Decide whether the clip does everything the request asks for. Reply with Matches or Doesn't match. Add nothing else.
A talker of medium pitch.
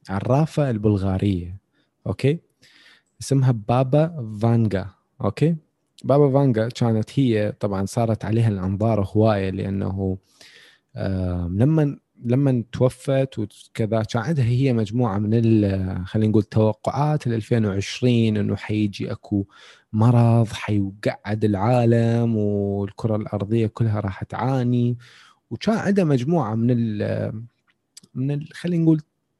Doesn't match